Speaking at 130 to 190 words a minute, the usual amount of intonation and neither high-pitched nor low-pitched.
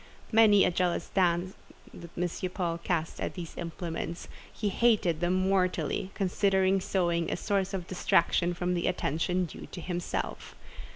No: average, 150 wpm; narrow, 1.8 semitones; medium, 180 Hz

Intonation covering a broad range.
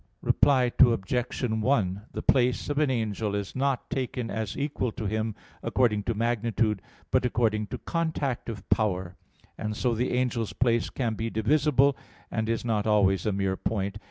No: average, 3.0 semitones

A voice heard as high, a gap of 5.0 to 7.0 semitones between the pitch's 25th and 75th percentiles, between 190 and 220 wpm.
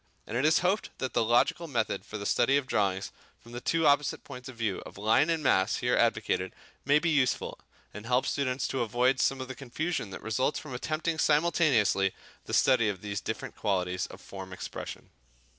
No: low, 125 Hz; wide, 5.4 semitones; average, 200 wpm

